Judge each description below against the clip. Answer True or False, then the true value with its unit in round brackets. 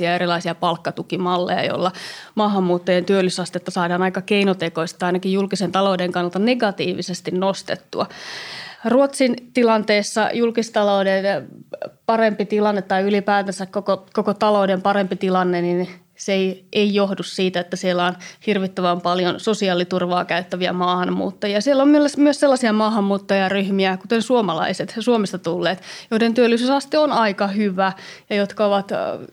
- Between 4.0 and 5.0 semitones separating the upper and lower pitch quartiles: False (2.9 semitones)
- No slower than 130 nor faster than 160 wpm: False (120 wpm)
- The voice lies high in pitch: True (195 Hz)